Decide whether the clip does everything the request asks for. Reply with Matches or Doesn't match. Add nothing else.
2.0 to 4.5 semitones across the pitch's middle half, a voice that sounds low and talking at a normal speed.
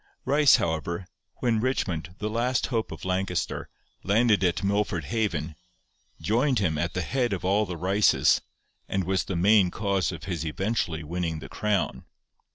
Matches